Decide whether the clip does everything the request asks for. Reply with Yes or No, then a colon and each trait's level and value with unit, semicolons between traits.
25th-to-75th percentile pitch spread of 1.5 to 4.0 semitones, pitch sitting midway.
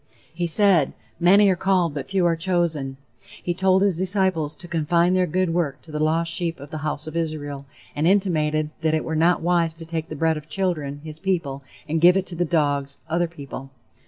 Yes: average, 2.7 semitones; medium, 165 Hz